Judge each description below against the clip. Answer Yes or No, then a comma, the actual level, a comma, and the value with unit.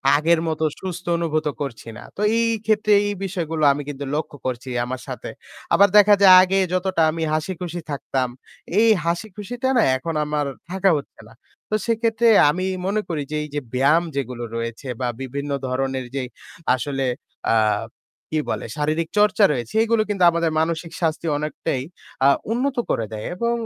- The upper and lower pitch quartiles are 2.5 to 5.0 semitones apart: No, wide, 5.6 semitones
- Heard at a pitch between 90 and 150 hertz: No, medium, 165 Hz